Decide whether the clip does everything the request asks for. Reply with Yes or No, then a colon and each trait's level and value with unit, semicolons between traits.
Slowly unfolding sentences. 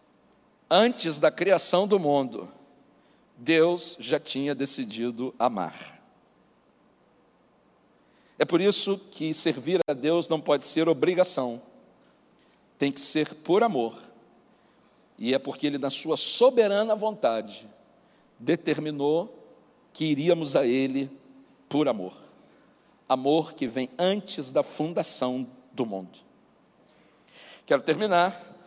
Yes: slow, 105 wpm